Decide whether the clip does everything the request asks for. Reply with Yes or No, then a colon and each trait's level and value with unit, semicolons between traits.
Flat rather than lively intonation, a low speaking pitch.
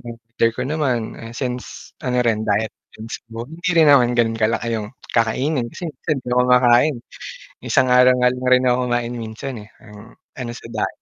Yes: narrow, 1.9 semitones; low, 125 Hz